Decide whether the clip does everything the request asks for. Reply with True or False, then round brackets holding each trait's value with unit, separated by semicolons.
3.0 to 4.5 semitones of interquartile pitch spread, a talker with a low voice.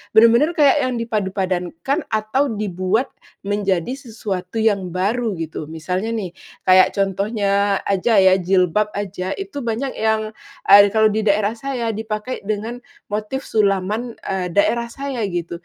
False (3.4 semitones; 210 Hz)